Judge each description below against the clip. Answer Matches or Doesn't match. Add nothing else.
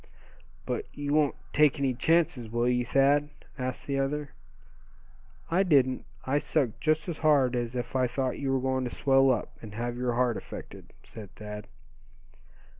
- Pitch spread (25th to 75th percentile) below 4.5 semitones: Matches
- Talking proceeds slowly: Doesn't match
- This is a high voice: Doesn't match